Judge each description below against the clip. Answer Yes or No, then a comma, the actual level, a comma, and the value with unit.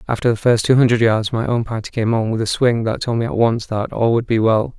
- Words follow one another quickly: Yes, fast, 300 wpm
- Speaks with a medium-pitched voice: No, low, 115 Hz